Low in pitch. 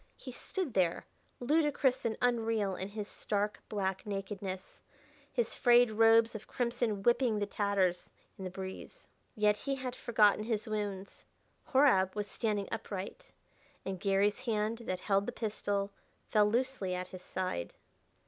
No: high, 210 Hz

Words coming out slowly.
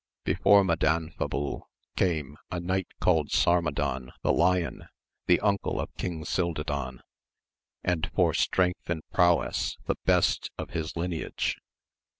Yes: slow, 120 wpm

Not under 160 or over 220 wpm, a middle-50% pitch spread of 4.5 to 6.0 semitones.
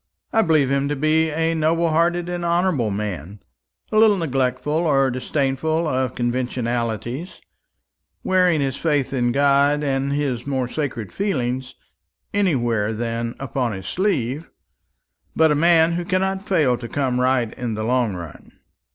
No: average, 145 wpm; average, 5.0 semitones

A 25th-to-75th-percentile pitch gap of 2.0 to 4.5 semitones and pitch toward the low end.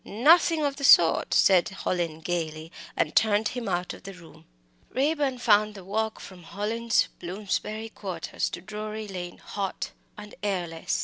No: average, 3.9 semitones; high, 205 Hz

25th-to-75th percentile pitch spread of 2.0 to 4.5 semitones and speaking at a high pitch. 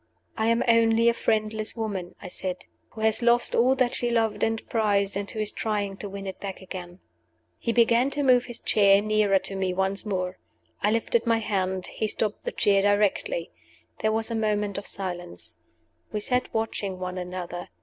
Yes: average, 2.8 semitones; high, 210 Hz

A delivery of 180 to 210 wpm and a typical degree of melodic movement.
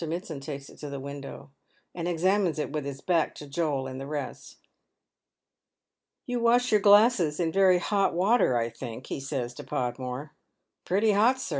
No: average, 185 wpm; wide, 6.1 semitones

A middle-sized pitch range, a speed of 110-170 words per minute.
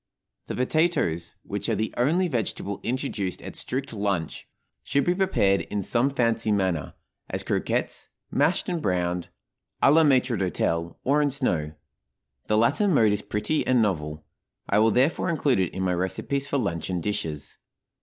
No: wide, 7.2 semitones; average, 160 wpm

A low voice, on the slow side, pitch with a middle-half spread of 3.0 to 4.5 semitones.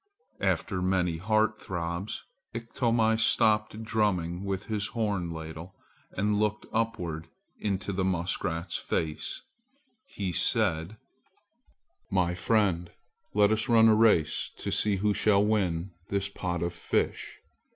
Yes: low, 100 Hz; slow, 120 wpm; average, 3.7 semitones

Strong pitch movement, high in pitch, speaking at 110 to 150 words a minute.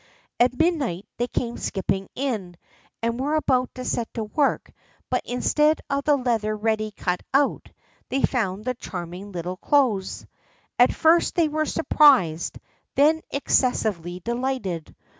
Yes: wide, 6.2 semitones; high, 240 Hz; average, 140 wpm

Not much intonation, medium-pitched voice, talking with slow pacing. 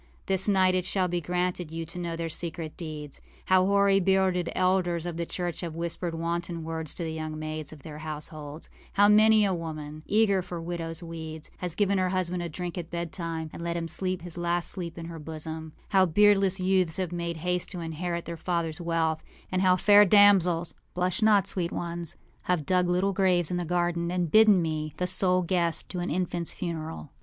No: narrow, 2.0 semitones; medium, 175 Hz; average, 200 wpm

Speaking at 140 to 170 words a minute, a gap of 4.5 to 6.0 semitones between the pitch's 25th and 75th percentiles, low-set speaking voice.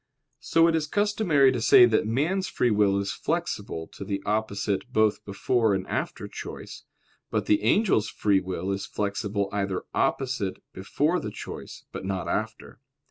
Yes: average, 160 wpm; wide, 5.5 semitones; low, 105 Hz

